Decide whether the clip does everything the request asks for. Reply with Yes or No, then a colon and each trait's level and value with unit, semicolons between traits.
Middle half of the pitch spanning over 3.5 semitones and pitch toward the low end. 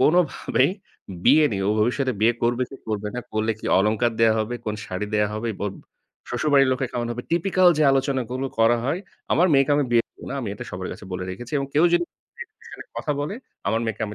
Yes: average, 4.3 semitones; low, 120 Hz